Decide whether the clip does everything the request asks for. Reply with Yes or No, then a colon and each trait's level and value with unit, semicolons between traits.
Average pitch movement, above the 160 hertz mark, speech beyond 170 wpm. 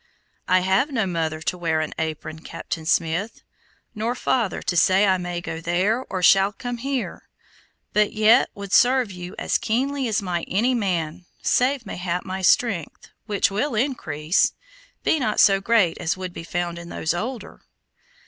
No: average, 4.9 semitones; high, 190 Hz; average, 165 wpm